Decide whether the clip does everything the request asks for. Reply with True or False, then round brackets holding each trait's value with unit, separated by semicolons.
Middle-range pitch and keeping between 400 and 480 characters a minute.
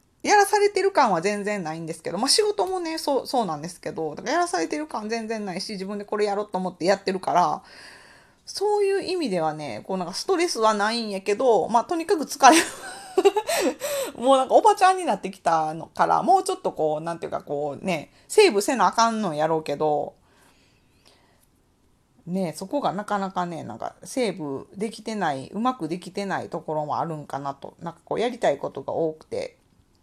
False (210 Hz; 405 characters per minute)